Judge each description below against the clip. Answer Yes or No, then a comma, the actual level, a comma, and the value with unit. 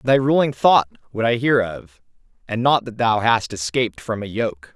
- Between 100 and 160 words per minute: No, average, 200 wpm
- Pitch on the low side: Yes, low, 115 Hz